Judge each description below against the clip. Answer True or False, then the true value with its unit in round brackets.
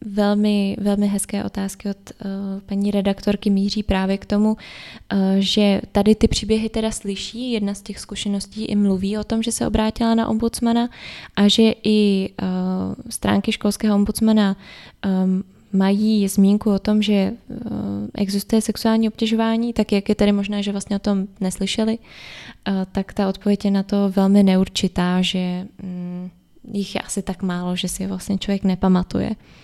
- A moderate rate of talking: True (150 wpm)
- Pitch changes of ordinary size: False (1.8 semitones)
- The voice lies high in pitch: True (200 Hz)